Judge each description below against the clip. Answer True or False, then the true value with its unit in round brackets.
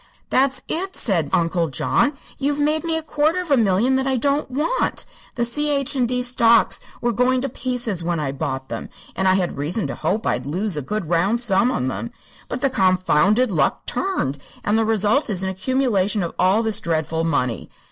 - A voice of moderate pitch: False (225 Hz)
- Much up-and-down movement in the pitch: True (6.8 semitones)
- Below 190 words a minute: False (200 wpm)